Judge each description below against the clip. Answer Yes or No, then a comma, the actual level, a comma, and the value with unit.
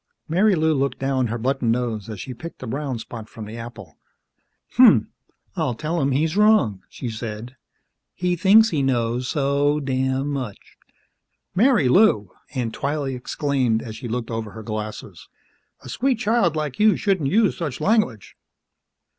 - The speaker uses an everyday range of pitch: No, wide, 5.7 semitones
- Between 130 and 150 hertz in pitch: Yes, low, 135 Hz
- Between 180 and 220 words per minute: No, average, 155 wpm